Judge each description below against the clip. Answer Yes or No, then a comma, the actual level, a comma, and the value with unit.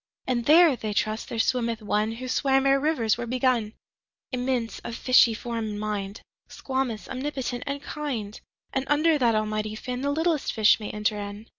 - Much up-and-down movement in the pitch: No, average, 3.8 semitones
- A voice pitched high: Yes, high, 240 Hz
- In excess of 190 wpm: No, average, 150 wpm